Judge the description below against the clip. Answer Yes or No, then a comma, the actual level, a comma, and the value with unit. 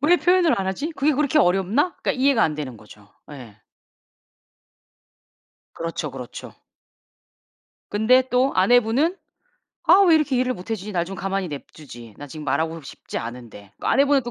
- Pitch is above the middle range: Yes, high, 195 Hz